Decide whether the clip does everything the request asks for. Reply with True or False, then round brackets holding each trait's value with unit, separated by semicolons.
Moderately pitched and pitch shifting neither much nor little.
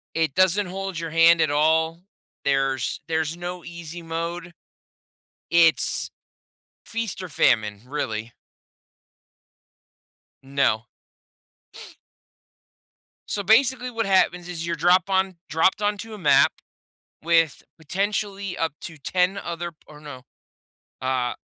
True (170 Hz; 3.8 semitones)